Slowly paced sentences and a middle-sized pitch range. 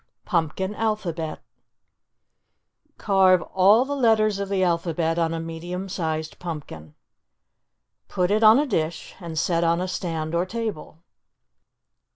Yes: slow, 130 wpm; average, 3.5 semitones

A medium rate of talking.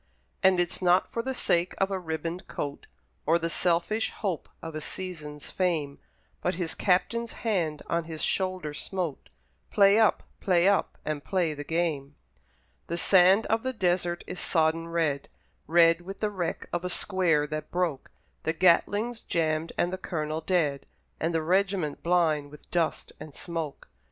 Yes: average, 165 wpm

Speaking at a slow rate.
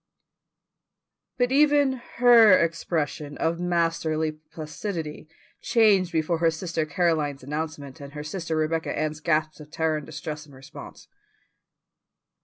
Yes: slow, 120 wpm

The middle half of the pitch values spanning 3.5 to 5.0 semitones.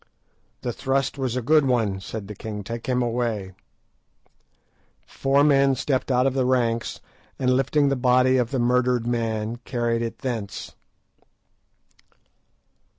No: narrow, 2.4 semitones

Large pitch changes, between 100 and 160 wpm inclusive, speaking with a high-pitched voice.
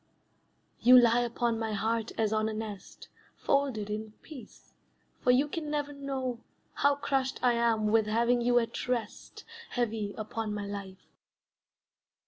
No: average, 2.8 semitones; average, 145 wpm; high, 230 Hz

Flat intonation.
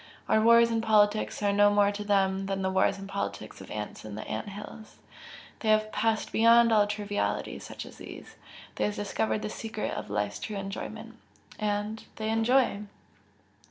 Yes: narrow, 1.7 semitones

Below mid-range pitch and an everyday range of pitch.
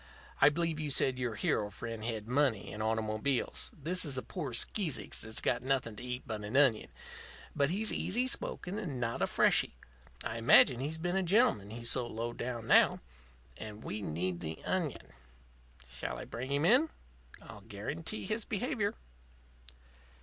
No: low, 125 Hz; wide, 7.0 semitones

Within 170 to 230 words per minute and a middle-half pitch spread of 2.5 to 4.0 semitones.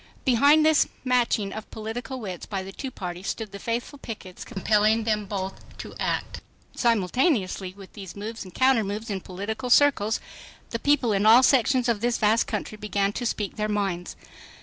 Yes: average, 175 wpm; average, 3.5 semitones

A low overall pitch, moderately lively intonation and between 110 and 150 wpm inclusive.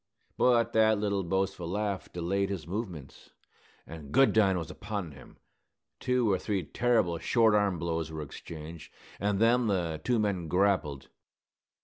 Yes: very low, 95 Hz; average, 4.3 semitones; average, 140 wpm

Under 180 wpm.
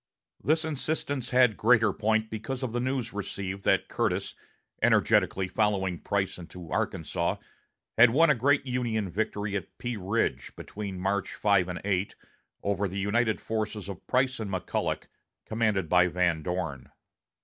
Yes: average, 150 wpm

